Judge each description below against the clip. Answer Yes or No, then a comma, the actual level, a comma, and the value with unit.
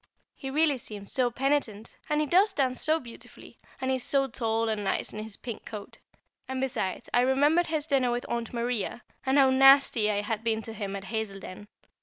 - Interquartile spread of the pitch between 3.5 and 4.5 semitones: Yes, average, 3.8 semitones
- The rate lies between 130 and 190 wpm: No, fast, 205 wpm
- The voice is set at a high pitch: Yes, high, 245 Hz